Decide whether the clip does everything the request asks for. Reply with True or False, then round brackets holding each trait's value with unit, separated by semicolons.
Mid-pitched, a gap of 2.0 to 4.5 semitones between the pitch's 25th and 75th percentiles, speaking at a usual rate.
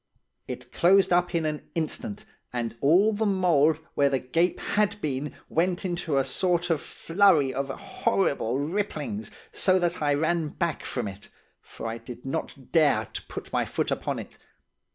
False (165 Hz; 5.0 semitones; 170 wpm)